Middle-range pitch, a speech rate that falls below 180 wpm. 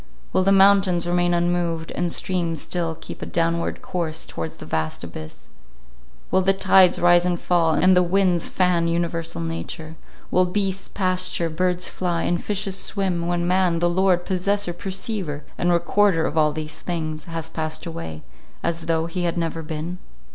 Yes: medium, 175 Hz; average, 170 wpm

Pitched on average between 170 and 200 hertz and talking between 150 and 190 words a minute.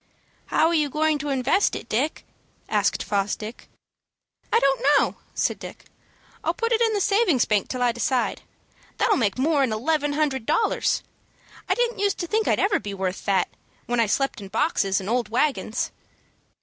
No: very high, 275 Hz; average, 175 wpm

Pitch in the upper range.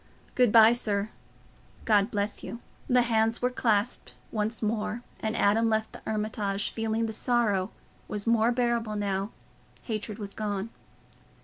Yes: high, 220 Hz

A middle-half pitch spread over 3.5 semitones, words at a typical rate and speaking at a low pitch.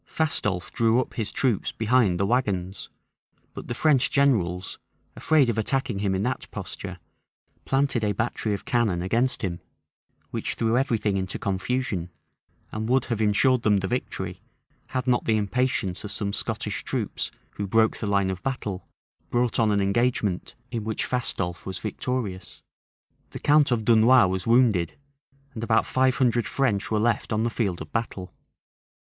Yes: average, 4.1 semitones; average, 165 wpm; low, 110 Hz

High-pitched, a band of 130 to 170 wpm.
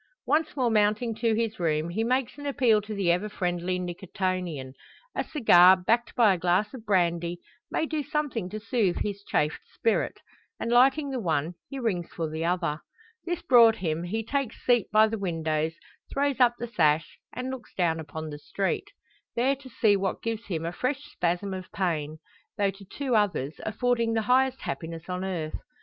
No: high, 205 Hz; average, 185 wpm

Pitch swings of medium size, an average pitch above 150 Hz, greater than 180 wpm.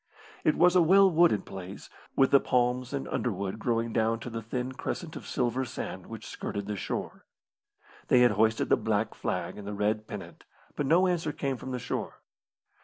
No: average, 5.0 semitones; low, 125 Hz; average, 190 wpm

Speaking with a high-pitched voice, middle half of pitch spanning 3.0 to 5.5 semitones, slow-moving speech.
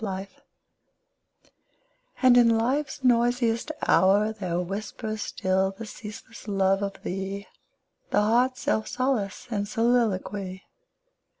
Yes: high, 215 Hz; average, 3.3 semitones; slow, 110 wpm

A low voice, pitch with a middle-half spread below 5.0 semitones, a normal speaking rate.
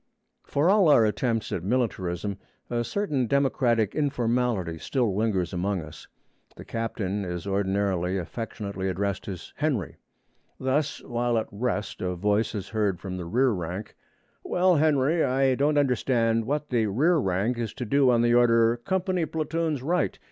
No: low, 115 Hz; wide, 5.5 semitones; average, 155 wpm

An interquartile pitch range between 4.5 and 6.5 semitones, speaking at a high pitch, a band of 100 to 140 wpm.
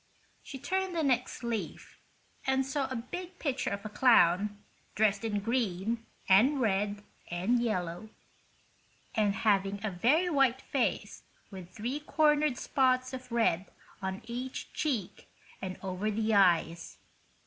Yes: average, 4.9 semitones; high, 230 Hz; slow, 135 wpm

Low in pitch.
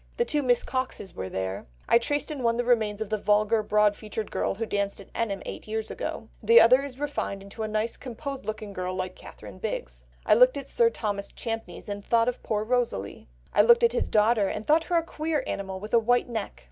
No: high, 220 Hz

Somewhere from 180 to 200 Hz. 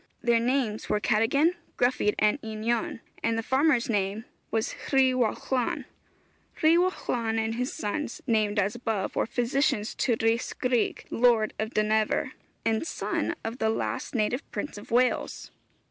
No: high, 230 Hz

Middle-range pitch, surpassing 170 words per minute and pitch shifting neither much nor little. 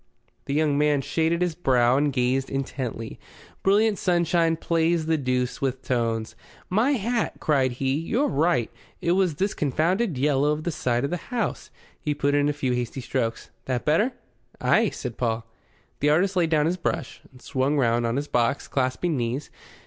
Yes: medium, 145 Hz; average, 180 wpm; average, 4.9 semitones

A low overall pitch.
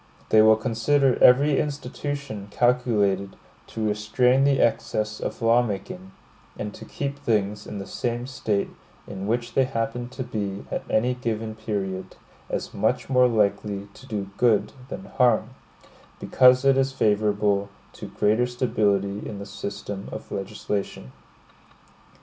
Yes: low, 110 Hz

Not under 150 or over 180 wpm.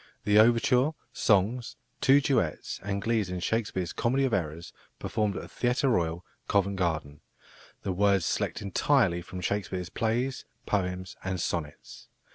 No: average, 140 wpm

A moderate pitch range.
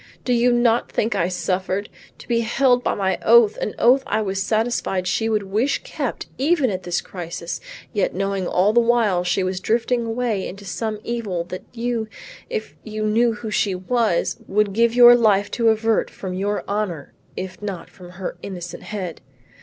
Yes: average, 3.8 semitones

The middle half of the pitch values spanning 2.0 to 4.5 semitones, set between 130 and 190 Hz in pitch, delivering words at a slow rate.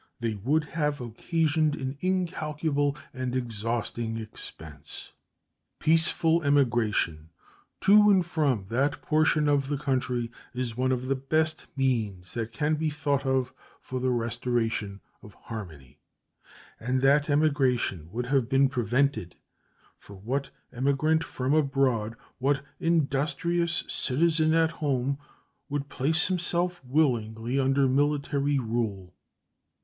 Yes: average, 4.2 semitones; low, 135 Hz; slow, 120 wpm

